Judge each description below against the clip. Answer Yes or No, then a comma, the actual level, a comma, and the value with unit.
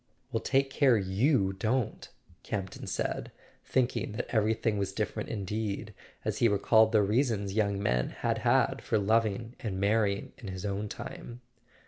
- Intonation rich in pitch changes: No, narrow, 2.4 semitones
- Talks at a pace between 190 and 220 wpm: No, average, 155 wpm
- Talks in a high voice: No, low, 105 Hz